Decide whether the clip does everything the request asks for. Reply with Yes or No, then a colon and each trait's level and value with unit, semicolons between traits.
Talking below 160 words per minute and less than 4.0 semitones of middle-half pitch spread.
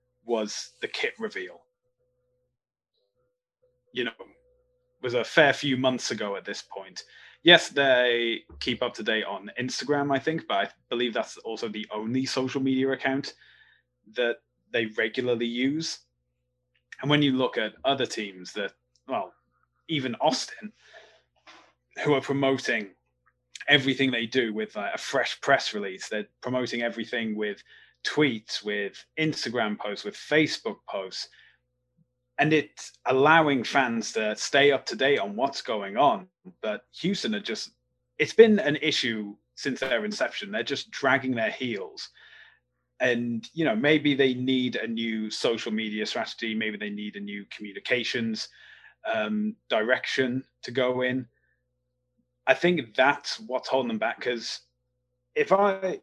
No: average, 145 wpm; average, 4.8 semitones